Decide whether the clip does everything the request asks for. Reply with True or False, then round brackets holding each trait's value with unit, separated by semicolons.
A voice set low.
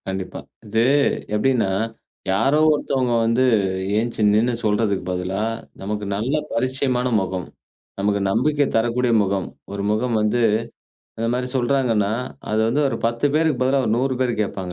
True (115 Hz)